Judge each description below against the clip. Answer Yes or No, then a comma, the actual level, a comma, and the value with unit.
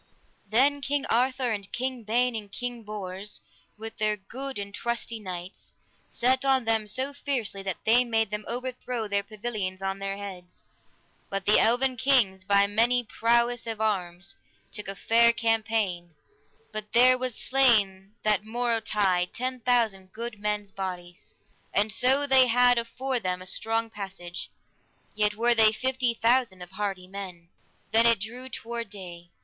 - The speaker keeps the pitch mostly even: No, average, 3.7 semitones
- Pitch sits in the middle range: No, high, 220 Hz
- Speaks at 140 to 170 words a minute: Yes, average, 155 wpm